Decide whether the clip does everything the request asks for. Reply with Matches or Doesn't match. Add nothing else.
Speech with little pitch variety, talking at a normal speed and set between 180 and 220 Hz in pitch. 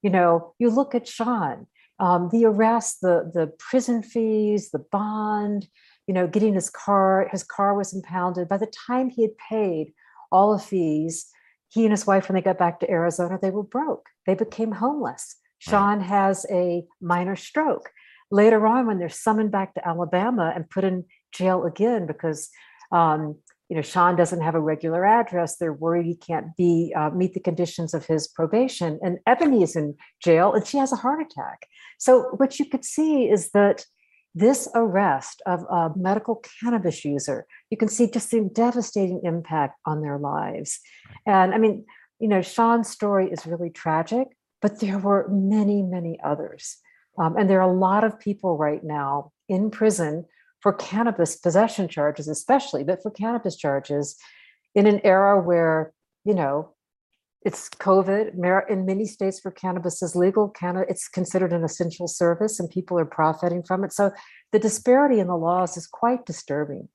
Doesn't match